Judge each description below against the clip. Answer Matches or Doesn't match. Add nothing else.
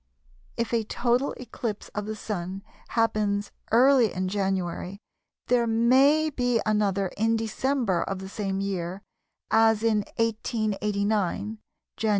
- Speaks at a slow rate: Matches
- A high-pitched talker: Matches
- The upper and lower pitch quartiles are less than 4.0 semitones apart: Matches